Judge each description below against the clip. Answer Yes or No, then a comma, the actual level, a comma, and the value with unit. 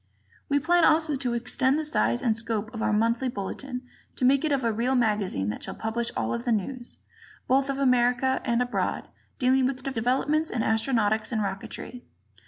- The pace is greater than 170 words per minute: Yes, average, 185 wpm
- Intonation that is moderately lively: Yes, average, 3.2 semitones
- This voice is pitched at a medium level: No, high, 245 Hz